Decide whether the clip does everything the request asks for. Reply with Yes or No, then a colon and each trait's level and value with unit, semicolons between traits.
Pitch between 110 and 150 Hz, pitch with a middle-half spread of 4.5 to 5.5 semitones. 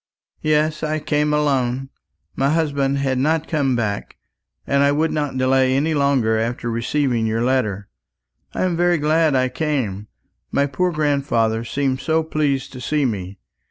No: medium, 140 Hz; average, 3.5 semitones